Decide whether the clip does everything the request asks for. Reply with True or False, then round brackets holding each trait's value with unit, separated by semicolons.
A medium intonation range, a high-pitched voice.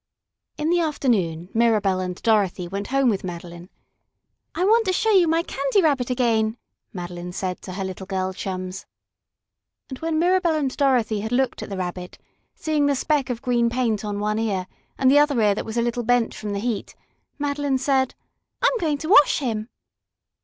False (6.6 semitones; 235 Hz)